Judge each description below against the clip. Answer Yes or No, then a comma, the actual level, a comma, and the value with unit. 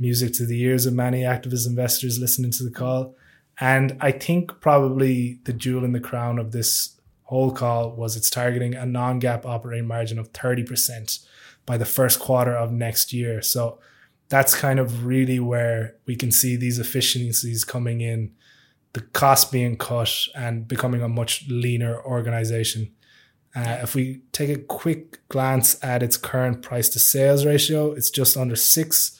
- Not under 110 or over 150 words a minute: No, average, 170 wpm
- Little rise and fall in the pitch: Yes, narrow, 1.8 semitones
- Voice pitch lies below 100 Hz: No, low, 125 Hz